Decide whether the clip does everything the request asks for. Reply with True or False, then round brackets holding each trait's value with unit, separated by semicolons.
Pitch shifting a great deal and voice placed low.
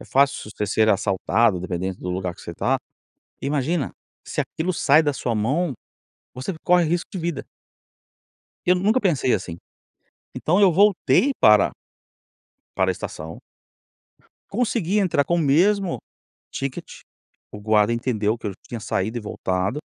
True (8.8 semitones; 130 Hz)